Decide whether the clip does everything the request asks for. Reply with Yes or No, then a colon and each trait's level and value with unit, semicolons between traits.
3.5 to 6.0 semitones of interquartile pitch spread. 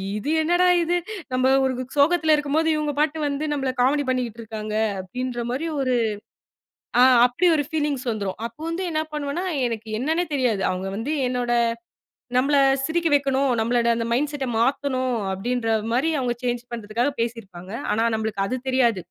Yes: average, 4.1 semitones